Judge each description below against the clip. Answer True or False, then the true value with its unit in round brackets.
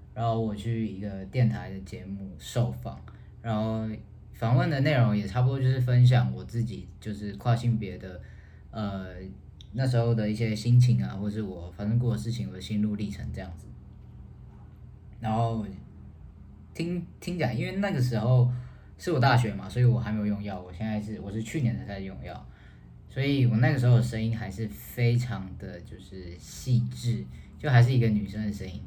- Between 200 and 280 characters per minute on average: True (270 characters per minute)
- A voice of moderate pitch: False (110 Hz)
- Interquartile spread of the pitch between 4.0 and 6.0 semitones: False (3.3 semitones)